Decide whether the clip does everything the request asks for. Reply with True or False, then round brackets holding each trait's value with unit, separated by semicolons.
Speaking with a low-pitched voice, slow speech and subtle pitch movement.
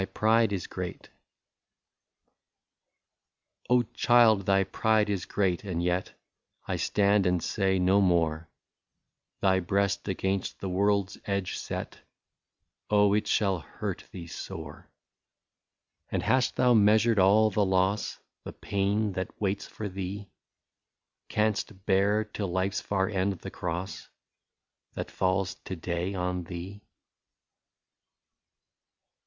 True (100 Hz; 125 wpm; 2.0 semitones)